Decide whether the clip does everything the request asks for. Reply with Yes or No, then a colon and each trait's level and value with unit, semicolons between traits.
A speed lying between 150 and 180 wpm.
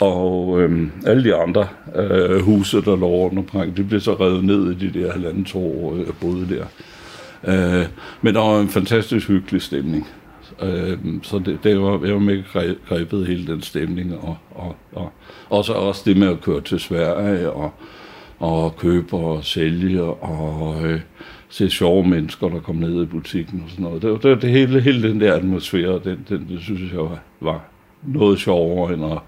No: average, 195 wpm